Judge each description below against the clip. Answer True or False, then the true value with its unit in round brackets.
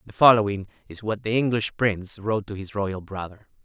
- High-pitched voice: False (105 Hz)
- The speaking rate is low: False (200 wpm)